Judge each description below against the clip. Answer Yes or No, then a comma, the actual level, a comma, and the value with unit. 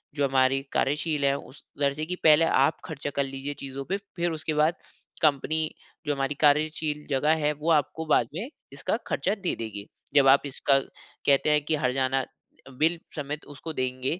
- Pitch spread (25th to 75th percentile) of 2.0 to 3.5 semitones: Yes, narrow, 2.5 semitones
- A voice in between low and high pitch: Yes, medium, 145 Hz